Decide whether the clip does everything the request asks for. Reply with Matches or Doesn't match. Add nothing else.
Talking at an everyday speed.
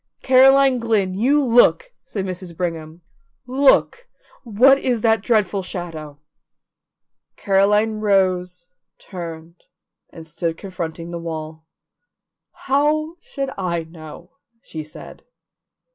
Doesn't match